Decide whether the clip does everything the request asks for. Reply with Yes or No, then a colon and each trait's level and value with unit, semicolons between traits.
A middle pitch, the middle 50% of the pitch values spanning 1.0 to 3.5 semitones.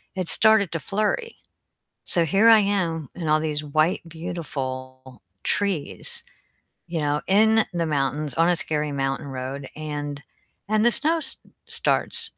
No: medium, 160 Hz; average, 5.3 semitones